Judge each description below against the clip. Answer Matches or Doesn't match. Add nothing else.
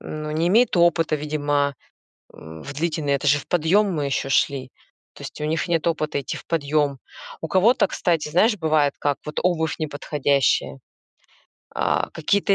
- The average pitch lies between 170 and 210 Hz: Doesn't match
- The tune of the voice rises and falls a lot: Doesn't match